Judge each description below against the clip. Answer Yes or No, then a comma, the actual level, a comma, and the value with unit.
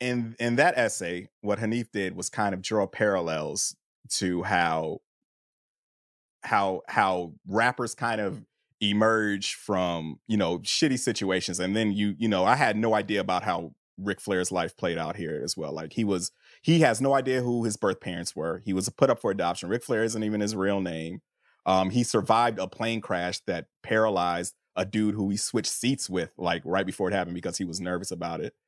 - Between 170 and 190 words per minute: No, average, 200 wpm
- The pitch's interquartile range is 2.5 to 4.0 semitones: Yes, average, 3.7 semitones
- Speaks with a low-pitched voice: Yes, low, 100 Hz